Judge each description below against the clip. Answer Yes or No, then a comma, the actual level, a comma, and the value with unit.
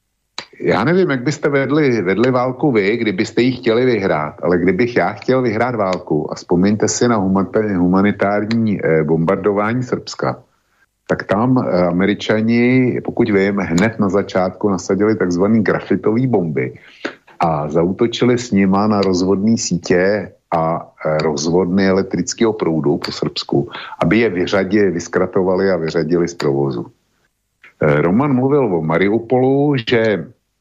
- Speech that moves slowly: No, average, 125 wpm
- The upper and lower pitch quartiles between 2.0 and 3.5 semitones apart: No, average, 4.9 semitones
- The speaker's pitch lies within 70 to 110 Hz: Yes, low, 105 Hz